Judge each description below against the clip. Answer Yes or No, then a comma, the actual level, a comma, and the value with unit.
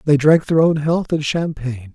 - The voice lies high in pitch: No, medium, 150 Hz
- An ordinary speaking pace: No, fast, 215 wpm